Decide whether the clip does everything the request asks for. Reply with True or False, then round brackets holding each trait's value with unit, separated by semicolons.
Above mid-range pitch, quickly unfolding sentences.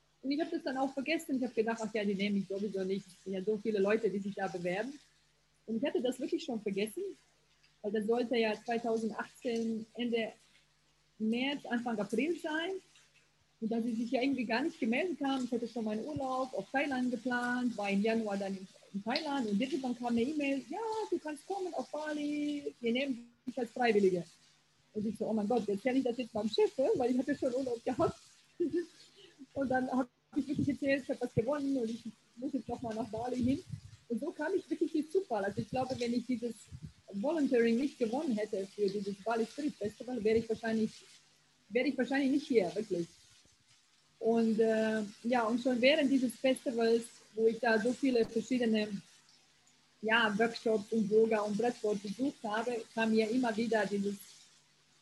True (240 Hz; 195 wpm)